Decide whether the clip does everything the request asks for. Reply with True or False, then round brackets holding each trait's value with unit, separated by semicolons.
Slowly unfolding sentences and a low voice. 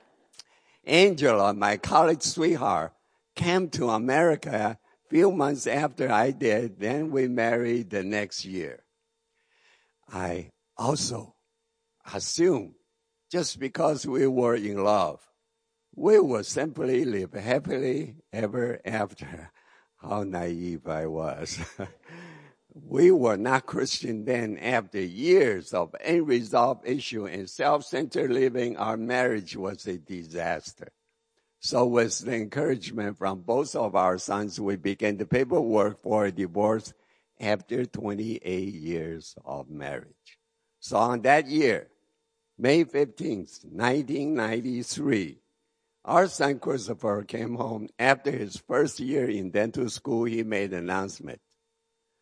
True (115 wpm; 120 Hz)